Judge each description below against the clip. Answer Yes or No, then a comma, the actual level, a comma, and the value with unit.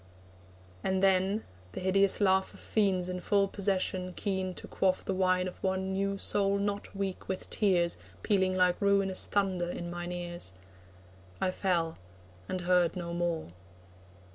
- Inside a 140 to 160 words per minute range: Yes, average, 150 wpm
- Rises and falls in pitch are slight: Yes, narrow, 1.6 semitones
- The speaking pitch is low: No, medium, 185 Hz